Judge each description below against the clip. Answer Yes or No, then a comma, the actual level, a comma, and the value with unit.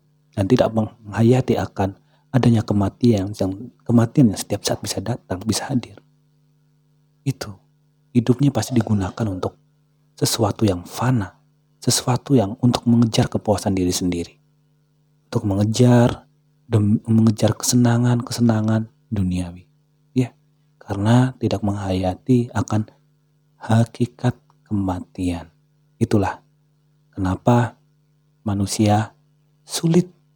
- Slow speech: No, average, 95 wpm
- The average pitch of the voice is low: Yes, low, 120 Hz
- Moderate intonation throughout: No, wide, 5.8 semitones